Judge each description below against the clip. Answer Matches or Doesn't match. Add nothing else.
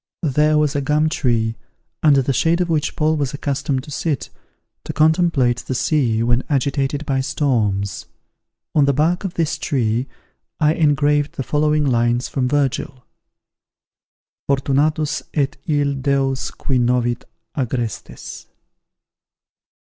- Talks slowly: Matches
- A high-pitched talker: Doesn't match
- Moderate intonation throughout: Matches